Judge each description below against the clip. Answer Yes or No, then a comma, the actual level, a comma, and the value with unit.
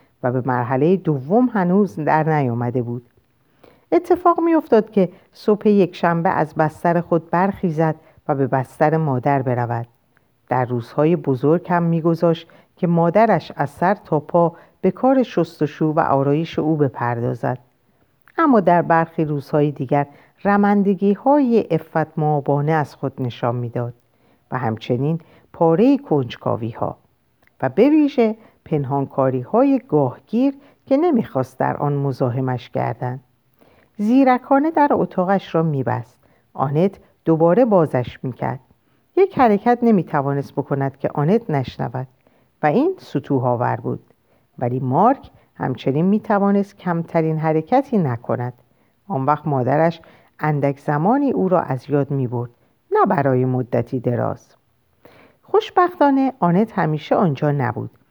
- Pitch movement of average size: No, wide, 6.9 semitones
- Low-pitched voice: No, medium, 155 Hz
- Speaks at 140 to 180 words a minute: No, average, 120 wpm